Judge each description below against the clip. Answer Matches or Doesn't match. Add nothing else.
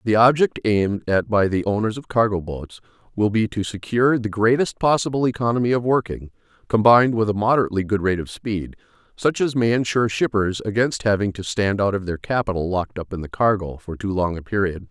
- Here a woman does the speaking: Doesn't match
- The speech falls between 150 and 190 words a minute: Doesn't match